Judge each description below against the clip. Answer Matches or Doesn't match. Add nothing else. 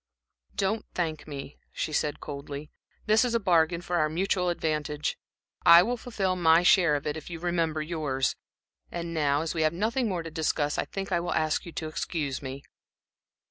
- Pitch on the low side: Doesn't match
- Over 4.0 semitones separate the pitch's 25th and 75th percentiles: Doesn't match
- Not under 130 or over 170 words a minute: Doesn't match